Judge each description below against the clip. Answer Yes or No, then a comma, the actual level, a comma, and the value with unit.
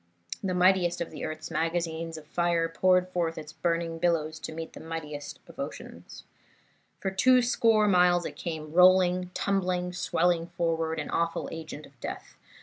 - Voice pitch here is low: No, medium, 170 Hz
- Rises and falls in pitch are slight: Yes, narrow, 1.9 semitones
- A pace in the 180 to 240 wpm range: No, average, 155 wpm